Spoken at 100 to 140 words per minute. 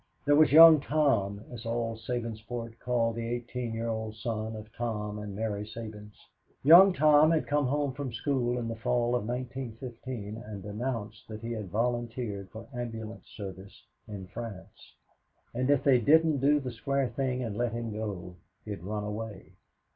No: average, 170 wpm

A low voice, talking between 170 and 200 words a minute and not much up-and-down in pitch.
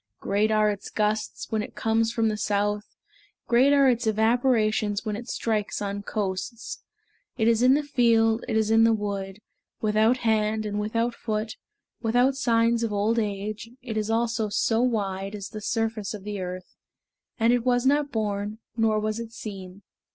No: high, 220 Hz; average, 175 wpm; narrow, 1.9 semitones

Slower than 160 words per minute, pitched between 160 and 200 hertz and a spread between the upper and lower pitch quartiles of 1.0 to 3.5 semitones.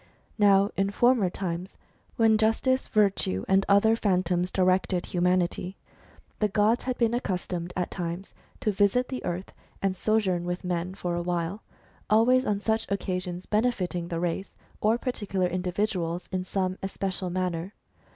Yes: average, 150 wpm; high, 190 Hz; average, 3.0 semitones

